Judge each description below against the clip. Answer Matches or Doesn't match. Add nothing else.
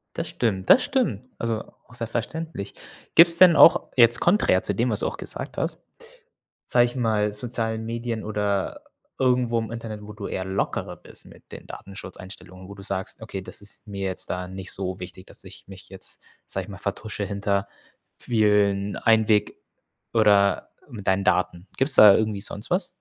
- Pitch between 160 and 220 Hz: Doesn't match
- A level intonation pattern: Doesn't match